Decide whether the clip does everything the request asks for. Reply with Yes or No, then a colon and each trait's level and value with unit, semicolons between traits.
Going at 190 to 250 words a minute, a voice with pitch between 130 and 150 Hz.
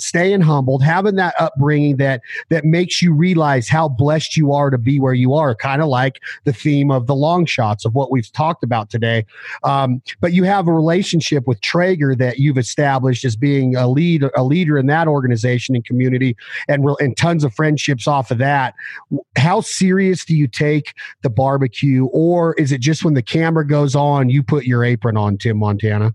Yes: average, 200 wpm; medium, 140 Hz